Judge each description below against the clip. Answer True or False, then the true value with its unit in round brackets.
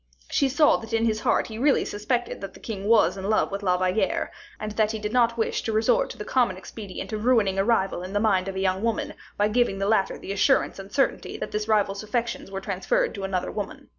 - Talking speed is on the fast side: True (245 wpm)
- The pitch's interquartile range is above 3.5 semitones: False (2.8 semitones)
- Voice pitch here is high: True (210 Hz)